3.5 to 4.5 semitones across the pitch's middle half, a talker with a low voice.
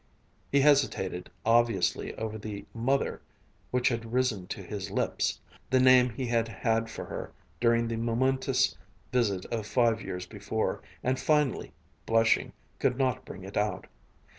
No: average, 3.1 semitones; low, 115 Hz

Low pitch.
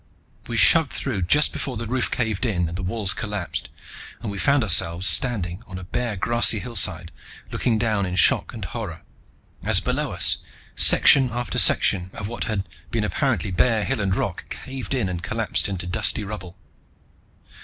Yes: low, 105 Hz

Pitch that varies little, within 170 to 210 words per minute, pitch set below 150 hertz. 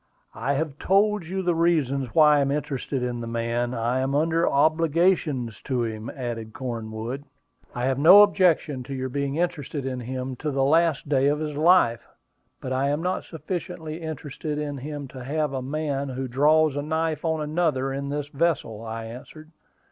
No: average, 3.6 semitones; average, 185 wpm; medium, 140 Hz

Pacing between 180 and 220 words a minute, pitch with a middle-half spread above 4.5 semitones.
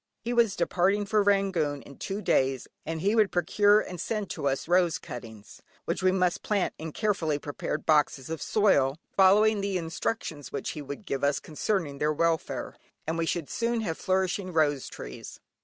Yes: average, 185 wpm; average, 5.3 semitones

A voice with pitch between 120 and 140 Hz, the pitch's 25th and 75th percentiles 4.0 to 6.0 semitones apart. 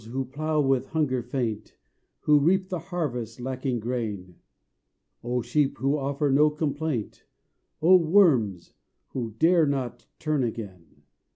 Yes: low, 135 Hz; average, 4.3 semitones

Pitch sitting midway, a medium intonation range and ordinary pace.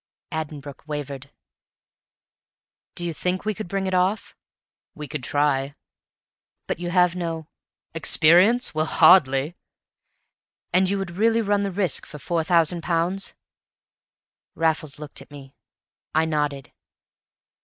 No: medium, 165 Hz; average, 3.7 semitones; slow, 130 wpm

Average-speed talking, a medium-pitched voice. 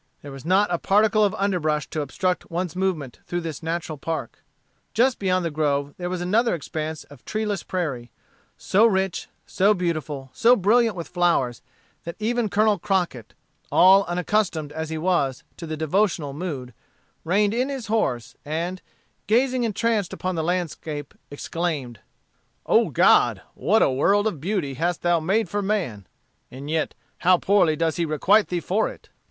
Yes: average, 165 wpm; medium, 175 Hz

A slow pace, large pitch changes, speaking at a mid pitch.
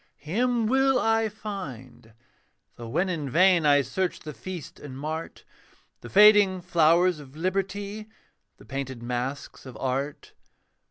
Yes: slow, 130 wpm; wide, 6.5 semitones; medium, 165 Hz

